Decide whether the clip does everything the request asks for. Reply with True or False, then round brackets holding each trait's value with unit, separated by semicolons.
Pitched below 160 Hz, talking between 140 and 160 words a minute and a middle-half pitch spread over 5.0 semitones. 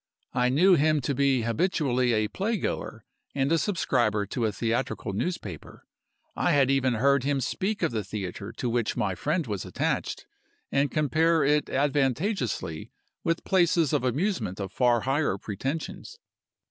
True (135 Hz; 155 wpm; 5.5 semitones)